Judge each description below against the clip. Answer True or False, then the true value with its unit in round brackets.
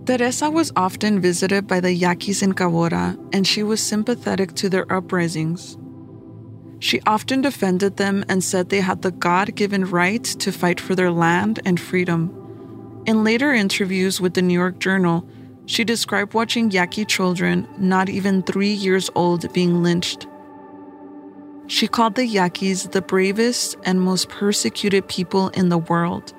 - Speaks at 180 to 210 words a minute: False (150 wpm)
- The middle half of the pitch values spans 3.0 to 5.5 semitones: False (2.5 semitones)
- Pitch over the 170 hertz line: True (190 Hz)